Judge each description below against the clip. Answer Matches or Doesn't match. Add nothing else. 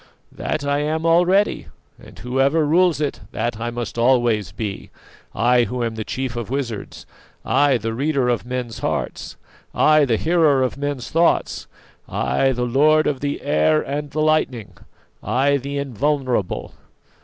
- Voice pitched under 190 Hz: Matches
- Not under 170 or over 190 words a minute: Doesn't match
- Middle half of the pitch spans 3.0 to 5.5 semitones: Matches